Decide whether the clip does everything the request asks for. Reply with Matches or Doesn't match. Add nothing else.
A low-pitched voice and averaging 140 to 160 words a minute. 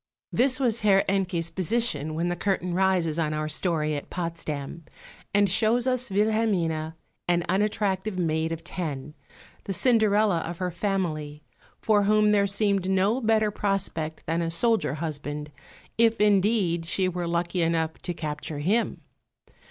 Doesn't match